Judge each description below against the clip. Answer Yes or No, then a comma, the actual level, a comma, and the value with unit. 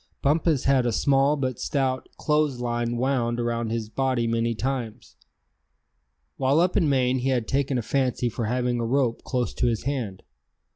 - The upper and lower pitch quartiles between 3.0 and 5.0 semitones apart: No, narrow, 2.5 semitones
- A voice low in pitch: Yes, low, 125 Hz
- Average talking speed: Yes, average, 175 wpm